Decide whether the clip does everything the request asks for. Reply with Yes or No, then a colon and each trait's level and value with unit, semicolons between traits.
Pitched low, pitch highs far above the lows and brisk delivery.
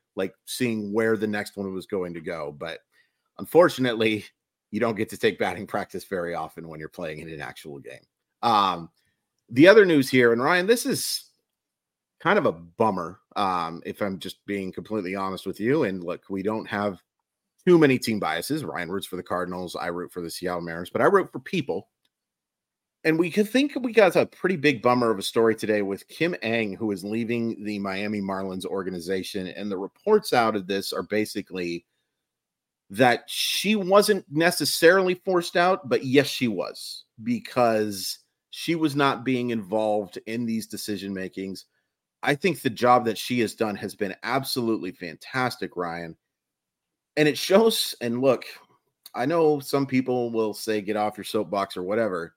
No: low, 110 Hz; wide, 6.3 semitones; average, 180 wpm